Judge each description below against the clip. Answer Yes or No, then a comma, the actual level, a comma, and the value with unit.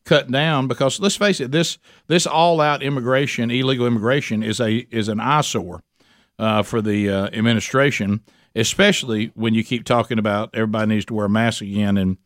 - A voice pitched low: Yes, low, 115 Hz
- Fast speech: No, average, 180 wpm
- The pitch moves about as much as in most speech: Yes, average, 3.9 semitones